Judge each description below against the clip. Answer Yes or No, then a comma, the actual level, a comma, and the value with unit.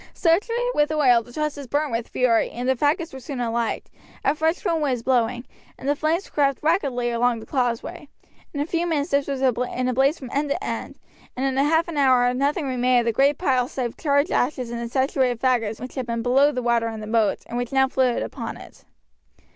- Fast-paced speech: Yes, fast, 225 wpm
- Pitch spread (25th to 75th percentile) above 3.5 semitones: No, average, 3.2 semitones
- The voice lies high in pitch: Yes, very high, 265 Hz